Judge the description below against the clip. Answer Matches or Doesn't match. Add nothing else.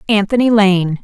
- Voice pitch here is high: Matches